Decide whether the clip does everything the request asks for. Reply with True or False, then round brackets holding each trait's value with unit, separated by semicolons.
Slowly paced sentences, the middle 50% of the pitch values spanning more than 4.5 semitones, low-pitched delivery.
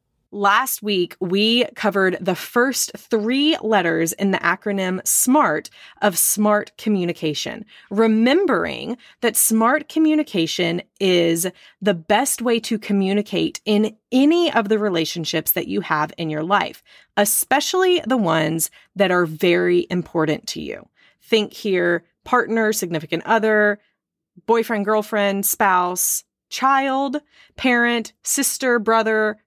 False (115 wpm; 4.9 semitones; 210 Hz)